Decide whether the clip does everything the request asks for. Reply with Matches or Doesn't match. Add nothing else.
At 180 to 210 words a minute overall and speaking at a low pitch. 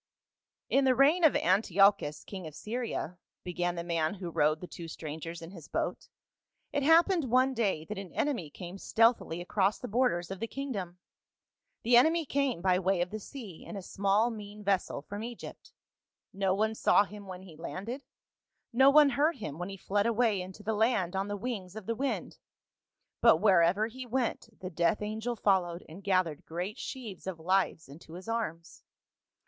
Doesn't match